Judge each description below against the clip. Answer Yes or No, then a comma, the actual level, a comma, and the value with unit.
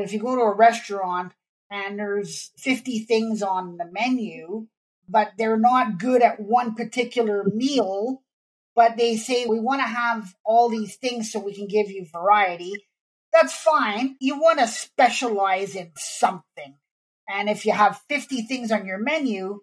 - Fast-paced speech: No, average, 165 wpm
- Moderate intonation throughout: Yes, average, 3.4 semitones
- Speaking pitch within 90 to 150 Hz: No, high, 220 Hz